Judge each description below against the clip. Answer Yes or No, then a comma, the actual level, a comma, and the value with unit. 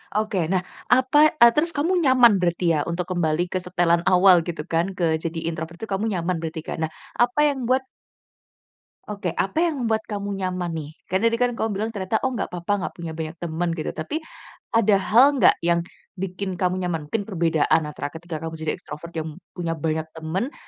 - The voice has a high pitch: No, medium, 180 Hz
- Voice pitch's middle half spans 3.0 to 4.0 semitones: No, average, 5.1 semitones